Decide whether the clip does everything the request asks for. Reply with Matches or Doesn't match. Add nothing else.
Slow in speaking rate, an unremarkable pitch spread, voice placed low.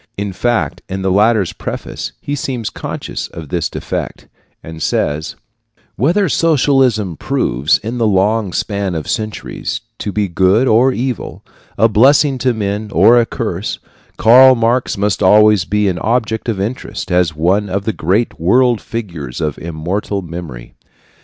Doesn't match